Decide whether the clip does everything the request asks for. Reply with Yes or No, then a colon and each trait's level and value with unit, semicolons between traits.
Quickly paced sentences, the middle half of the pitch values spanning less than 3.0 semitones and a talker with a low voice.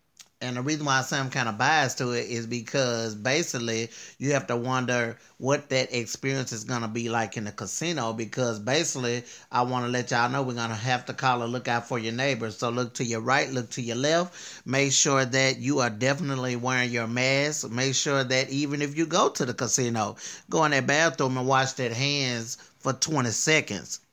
Yes: fast, 215 wpm; narrow, 2.4 semitones; low, 125 Hz